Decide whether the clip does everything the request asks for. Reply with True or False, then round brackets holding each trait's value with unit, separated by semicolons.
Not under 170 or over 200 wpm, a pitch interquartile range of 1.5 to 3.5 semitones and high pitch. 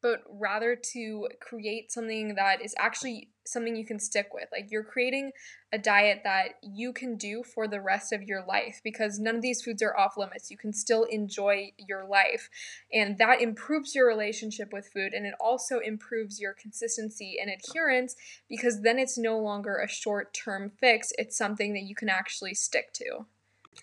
True (185 wpm; 2.8 semitones; 220 Hz)